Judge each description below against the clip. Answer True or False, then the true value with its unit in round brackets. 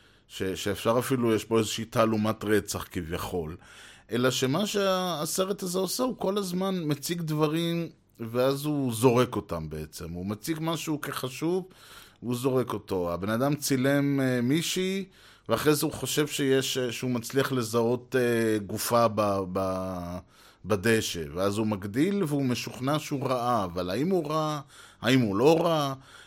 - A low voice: True (125 Hz)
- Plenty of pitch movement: True (6.1 semitones)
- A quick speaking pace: False (140 wpm)